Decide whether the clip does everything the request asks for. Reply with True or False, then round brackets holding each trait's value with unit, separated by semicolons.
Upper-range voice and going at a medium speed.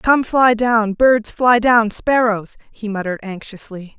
True (225 Hz; 150 wpm)